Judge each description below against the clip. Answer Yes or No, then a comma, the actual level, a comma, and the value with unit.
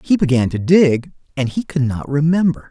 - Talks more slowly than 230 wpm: Yes, average, 200 wpm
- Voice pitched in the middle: Yes, medium, 145 Hz